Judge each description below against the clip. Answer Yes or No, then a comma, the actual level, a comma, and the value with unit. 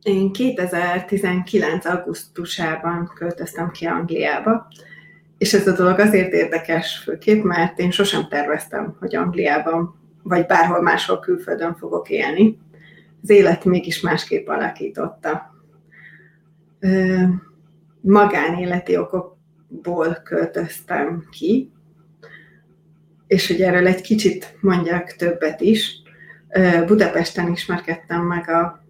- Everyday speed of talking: No, slow, 95 wpm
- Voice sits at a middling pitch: Yes, medium, 175 Hz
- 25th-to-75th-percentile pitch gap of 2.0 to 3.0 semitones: Yes, average, 2.7 semitones